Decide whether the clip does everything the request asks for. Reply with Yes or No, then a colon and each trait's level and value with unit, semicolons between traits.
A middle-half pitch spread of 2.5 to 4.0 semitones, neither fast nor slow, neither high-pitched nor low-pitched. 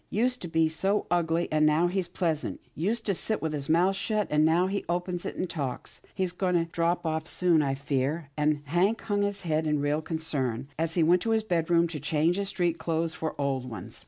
No: average, 3.0 semitones; fast, 225 wpm; medium, 165 Hz